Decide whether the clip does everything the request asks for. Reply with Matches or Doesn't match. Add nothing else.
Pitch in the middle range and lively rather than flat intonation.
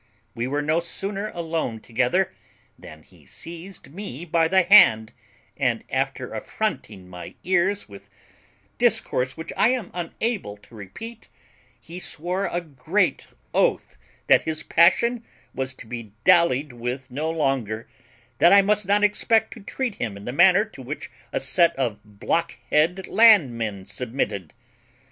Matches